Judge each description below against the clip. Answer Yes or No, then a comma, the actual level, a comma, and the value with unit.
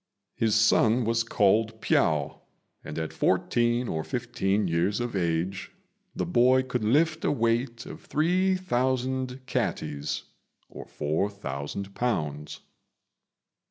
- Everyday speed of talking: No, slow, 110 wpm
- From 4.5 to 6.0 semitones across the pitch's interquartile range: Yes, average, 5.1 semitones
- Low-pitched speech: Yes, low, 115 Hz